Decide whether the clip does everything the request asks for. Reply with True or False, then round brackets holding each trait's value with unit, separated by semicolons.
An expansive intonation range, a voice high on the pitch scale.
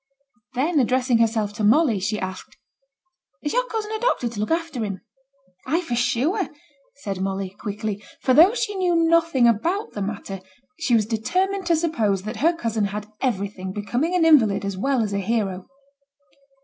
True (8.2 semitones; 235 Hz)